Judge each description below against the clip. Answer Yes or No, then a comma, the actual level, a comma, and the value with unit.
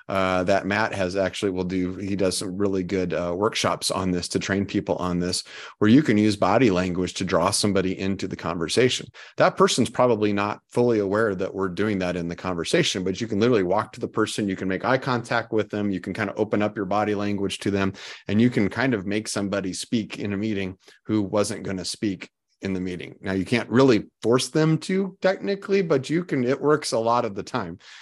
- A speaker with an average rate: No, fast, 235 wpm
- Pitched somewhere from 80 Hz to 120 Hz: Yes, low, 100 Hz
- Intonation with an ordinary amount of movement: Yes, average, 3.7 semitones